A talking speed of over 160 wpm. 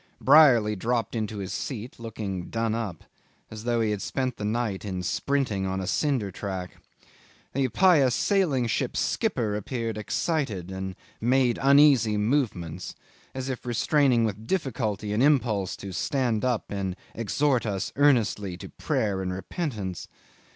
No: average, 145 wpm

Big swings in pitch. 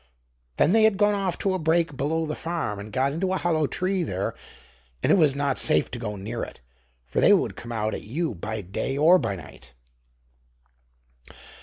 Yes: wide, 8.0 semitones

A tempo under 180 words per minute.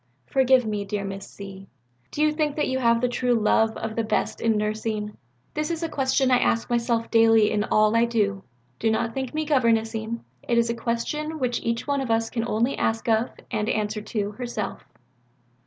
No: fast, 205 wpm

